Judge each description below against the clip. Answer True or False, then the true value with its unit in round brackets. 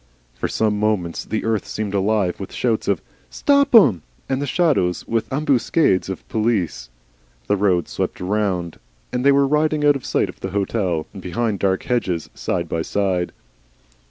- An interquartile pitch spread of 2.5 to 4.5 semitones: False (5.4 semitones)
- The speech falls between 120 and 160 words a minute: False (170 wpm)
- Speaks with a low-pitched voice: True (105 Hz)